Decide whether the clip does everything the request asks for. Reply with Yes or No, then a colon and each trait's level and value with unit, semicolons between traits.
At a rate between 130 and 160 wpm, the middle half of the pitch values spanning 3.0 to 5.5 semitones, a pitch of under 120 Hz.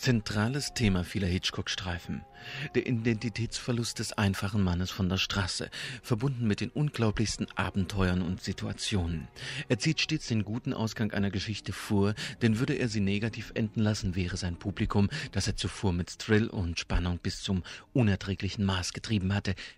Yes: average, 155 wpm; average, 3.6 semitones; low, 105 Hz